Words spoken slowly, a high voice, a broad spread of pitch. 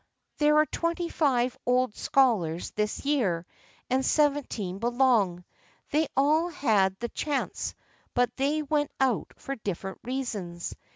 Yes: slow, 125 wpm; very high, 255 Hz; wide, 6.0 semitones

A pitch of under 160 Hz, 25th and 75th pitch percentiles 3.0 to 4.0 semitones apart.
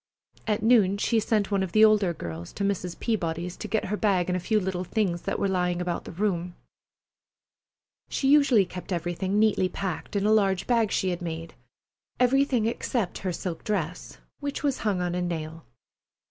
No: high, 190 Hz; average, 3.5 semitones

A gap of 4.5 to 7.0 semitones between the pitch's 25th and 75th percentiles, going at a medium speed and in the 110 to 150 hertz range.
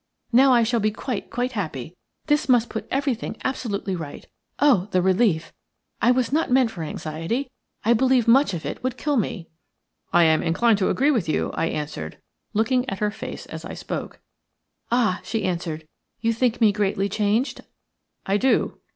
No: wide, 5.5 semitones; average, 175 wpm; high, 220 Hz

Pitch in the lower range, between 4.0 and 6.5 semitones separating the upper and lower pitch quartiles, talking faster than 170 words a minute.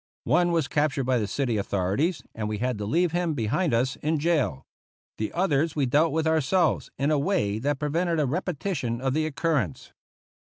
No: medium, 145 Hz; average, 5.3 semitones; average, 195 wpm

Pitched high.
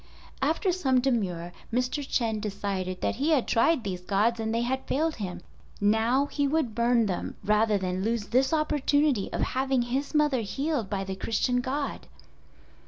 Yes: high, 235 Hz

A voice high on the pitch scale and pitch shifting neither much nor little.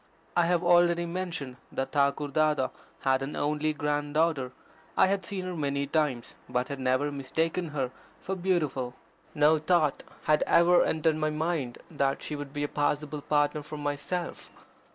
No: medium, 150 Hz; average, 3.1 semitones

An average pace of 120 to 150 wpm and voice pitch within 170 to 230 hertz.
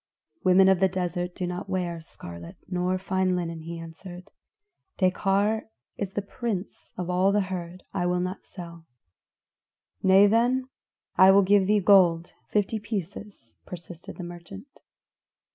Yes: average, 145 wpm; medium, 185 Hz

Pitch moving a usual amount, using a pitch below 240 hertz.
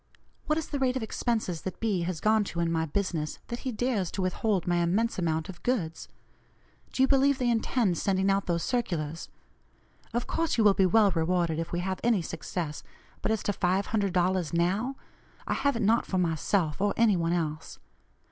Yes: average, 5.0 semitones; high, 190 Hz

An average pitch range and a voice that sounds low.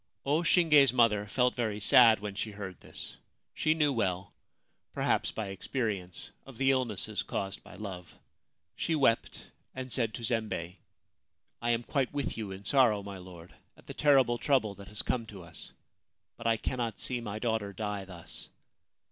Yes: average, 4.2 semitones; low, 110 Hz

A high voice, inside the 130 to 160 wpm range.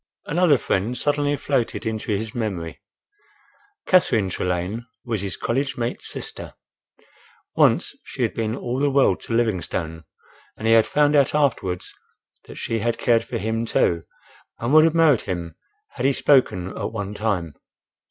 No: low, 115 Hz; average, 155 wpm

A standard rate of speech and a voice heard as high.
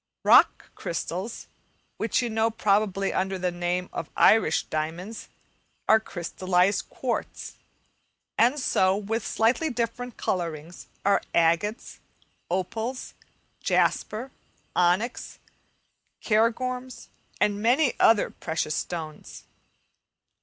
No: slow, 95 wpm; high, 205 Hz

